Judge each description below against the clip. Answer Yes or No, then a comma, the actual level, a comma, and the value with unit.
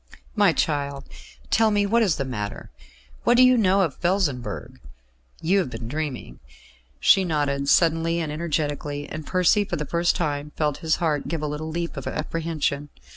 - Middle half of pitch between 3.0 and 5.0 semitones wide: Yes, average, 3.5 semitones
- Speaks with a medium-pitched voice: Yes, medium, 155 Hz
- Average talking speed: Yes, average, 175 wpm